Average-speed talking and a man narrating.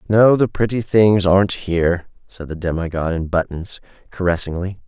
Yes: average, 160 wpm; male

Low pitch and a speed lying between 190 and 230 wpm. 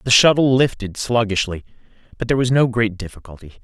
No: low, 115 Hz; average, 165 wpm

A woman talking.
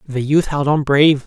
No: male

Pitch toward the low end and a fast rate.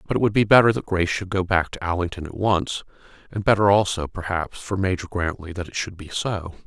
Yes: very low, 95 Hz; fast, 235 wpm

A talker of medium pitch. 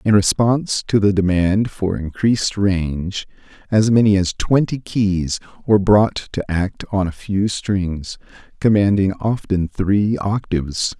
No: low, 100 Hz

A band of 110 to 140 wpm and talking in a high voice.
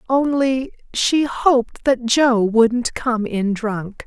Yes: slow, 135 wpm; high, 240 Hz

